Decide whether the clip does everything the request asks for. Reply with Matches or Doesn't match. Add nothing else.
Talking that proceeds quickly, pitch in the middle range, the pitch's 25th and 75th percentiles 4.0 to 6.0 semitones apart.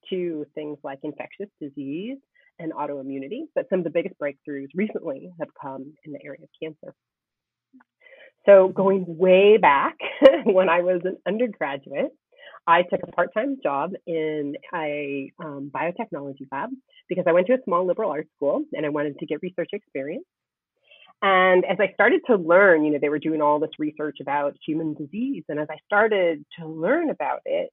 Doesn't match